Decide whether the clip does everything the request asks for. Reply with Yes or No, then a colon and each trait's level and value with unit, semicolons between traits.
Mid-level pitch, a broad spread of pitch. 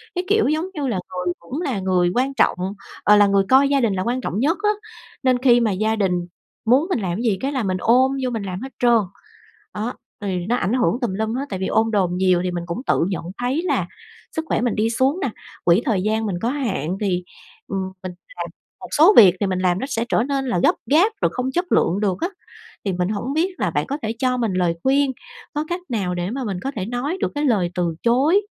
No: high, 225 Hz; wide, 6.0 semitones